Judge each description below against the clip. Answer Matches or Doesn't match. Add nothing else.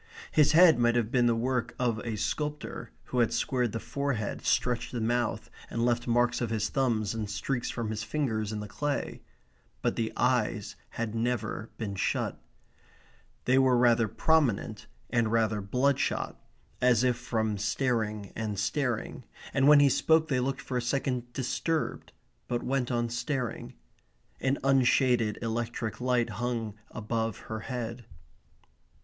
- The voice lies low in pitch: Matches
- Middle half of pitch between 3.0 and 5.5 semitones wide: Doesn't match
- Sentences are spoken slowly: Doesn't match